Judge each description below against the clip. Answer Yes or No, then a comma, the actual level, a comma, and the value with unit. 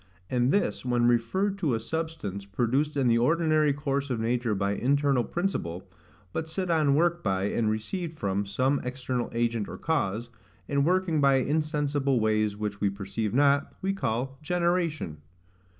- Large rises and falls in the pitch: Yes, wide, 5.9 semitones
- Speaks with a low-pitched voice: Yes, low, 130 Hz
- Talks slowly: No, average, 160 wpm